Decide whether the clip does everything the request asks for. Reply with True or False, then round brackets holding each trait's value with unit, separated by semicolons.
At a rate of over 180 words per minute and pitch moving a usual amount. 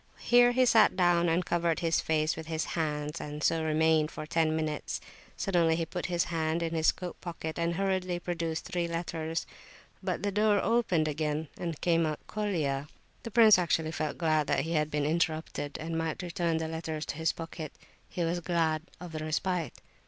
False (190 wpm; 2.0 semitones)